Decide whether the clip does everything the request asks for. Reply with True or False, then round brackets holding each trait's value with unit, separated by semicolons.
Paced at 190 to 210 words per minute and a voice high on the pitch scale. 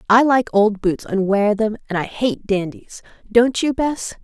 True (200 wpm; 220 Hz)